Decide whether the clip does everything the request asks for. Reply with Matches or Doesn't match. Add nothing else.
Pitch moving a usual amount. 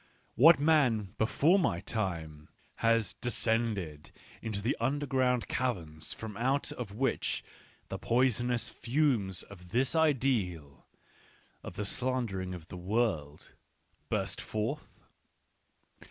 Doesn't match